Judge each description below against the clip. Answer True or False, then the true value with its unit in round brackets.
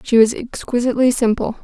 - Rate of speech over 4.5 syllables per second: True (5.9 syllables/s)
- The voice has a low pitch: False (240 Hz)